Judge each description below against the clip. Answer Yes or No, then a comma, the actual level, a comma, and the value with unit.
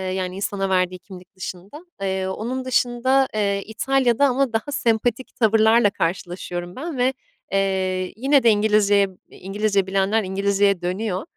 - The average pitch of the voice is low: No, high, 205 Hz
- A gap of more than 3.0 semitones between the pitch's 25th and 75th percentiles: Yes, average, 4.0 semitones